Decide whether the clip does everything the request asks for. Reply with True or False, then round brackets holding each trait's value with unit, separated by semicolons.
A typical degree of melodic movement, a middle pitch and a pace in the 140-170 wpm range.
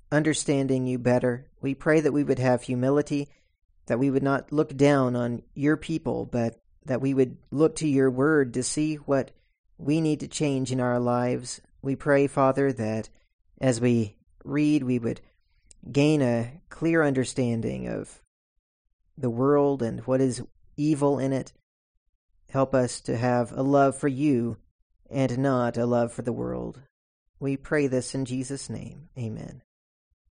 False (3.4 semitones; 130 Hz; 160 wpm)